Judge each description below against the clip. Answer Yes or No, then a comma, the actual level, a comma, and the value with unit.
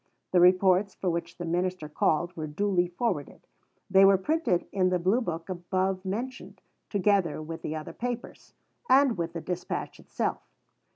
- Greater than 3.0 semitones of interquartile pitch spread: No, narrow, 2.6 semitones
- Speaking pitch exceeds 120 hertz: Yes, medium, 185 Hz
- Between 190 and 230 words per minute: No, average, 160 wpm